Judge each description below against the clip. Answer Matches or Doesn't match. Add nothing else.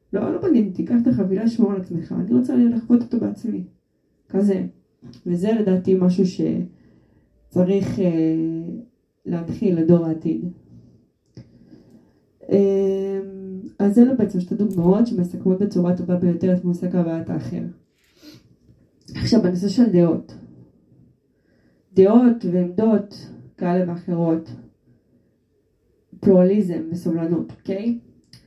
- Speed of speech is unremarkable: Doesn't match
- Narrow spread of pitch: Doesn't match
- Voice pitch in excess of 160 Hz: Matches